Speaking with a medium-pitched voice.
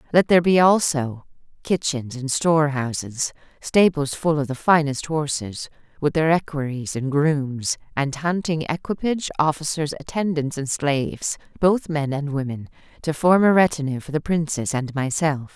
Yes: medium, 150 Hz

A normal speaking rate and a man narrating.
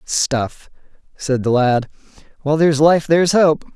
Yes: average, 145 wpm; male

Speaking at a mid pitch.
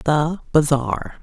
Yes: medium, 155 Hz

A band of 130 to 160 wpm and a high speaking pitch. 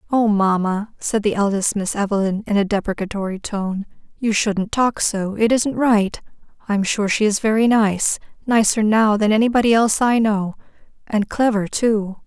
Yes: average, 150 wpm; high, 210 Hz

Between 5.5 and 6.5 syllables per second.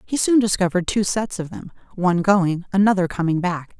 Yes: 5.7 syllables/s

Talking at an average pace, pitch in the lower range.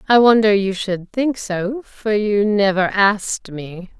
No: average, 165 wpm; high, 205 Hz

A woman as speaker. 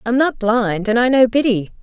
Yes: female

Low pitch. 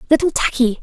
No: very high, 265 Hz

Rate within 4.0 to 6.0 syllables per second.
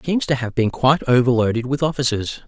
No: 6.6 syllables/s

